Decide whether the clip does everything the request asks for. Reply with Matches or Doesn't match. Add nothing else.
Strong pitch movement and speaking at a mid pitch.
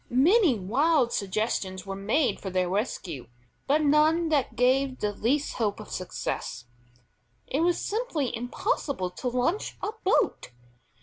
Doesn't match